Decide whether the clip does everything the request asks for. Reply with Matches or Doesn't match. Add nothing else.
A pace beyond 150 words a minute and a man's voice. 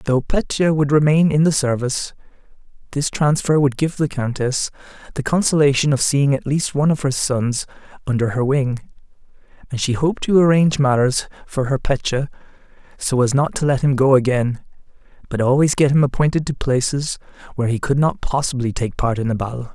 Matches